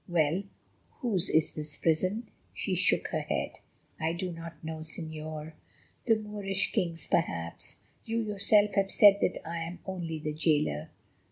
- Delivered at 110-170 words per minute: Yes, average, 145 wpm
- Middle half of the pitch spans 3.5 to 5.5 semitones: Yes, average, 3.9 semitones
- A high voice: No, medium, 170 Hz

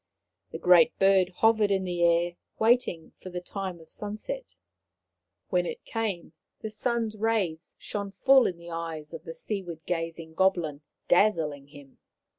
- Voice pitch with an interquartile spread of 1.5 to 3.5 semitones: No, average, 4.3 semitones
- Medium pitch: Yes, medium, 180 Hz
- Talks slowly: No, average, 150 wpm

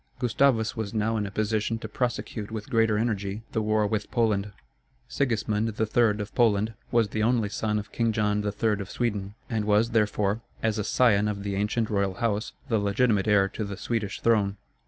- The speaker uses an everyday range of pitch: No, narrow, 1.7 semitones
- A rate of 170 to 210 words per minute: Yes, average, 190 wpm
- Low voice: Yes, low, 105 Hz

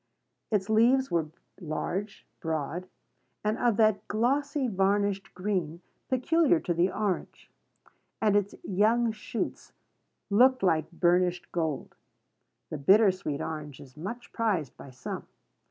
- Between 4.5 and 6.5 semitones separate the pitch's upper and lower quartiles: Yes, average, 4.8 semitones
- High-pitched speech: Yes, high, 195 Hz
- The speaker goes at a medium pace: No, slow, 120 wpm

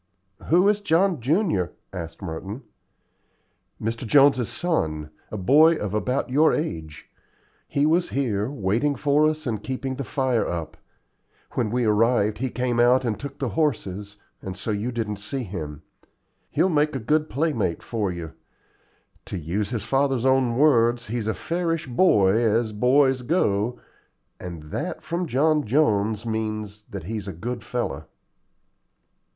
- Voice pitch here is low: Yes, low, 120 Hz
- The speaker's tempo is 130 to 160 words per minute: Yes, average, 150 wpm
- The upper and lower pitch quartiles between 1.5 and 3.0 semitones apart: No, wide, 5.5 semitones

